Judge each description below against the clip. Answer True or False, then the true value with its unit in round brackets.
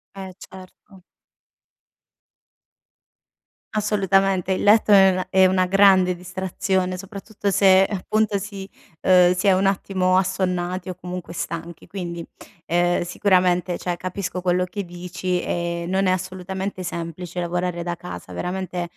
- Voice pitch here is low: False (185 Hz)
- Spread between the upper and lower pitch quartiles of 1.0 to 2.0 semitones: True (1.4 semitones)